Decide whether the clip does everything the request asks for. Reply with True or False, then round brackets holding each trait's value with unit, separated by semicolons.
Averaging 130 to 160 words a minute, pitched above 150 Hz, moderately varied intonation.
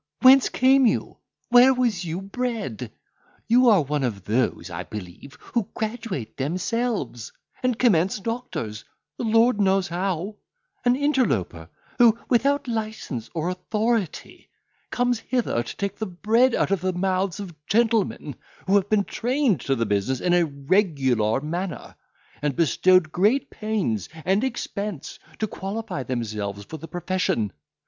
False (140 wpm; 190 Hz; 8.4 semitones)